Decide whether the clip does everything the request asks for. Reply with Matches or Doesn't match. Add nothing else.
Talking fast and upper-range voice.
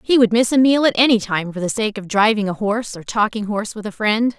Matches